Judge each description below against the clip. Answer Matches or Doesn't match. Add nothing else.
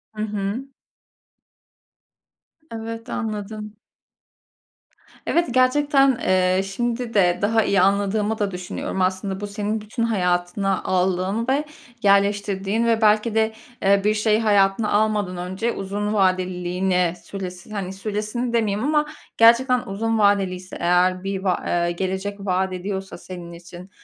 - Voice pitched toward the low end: Doesn't match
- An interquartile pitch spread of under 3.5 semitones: Matches